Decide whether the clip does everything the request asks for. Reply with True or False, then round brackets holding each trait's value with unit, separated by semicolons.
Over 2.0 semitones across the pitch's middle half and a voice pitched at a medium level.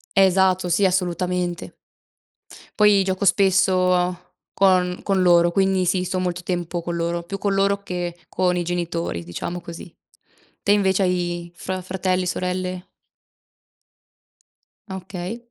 False (1.5 semitones; 180 Hz)